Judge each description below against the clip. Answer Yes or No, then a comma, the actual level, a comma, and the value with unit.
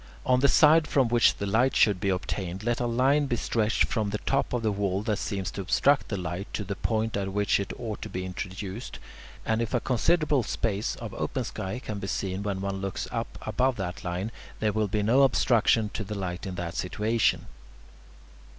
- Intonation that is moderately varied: Yes, average, 3.6 semitones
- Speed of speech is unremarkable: No, fast, 215 wpm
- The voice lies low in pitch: Yes, low, 105 Hz